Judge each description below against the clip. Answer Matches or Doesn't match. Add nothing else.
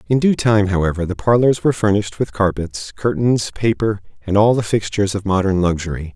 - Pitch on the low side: Matches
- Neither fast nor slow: Matches